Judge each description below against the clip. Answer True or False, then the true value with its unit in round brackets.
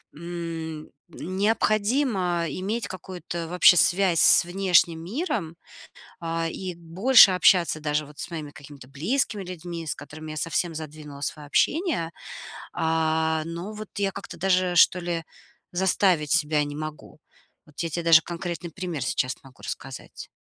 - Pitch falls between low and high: True (170 Hz)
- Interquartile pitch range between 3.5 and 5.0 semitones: False (3.0 semitones)